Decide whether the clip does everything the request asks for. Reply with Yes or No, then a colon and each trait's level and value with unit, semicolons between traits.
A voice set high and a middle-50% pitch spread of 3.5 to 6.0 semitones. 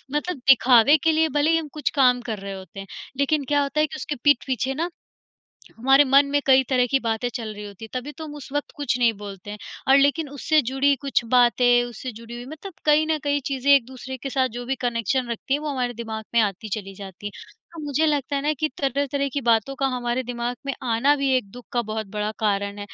Yes: very high, 260 Hz; average, 3.8 semitones